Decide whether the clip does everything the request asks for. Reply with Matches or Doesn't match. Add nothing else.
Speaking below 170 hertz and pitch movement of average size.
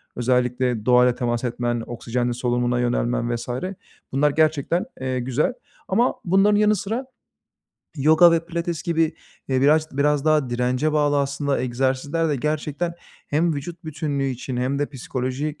Matches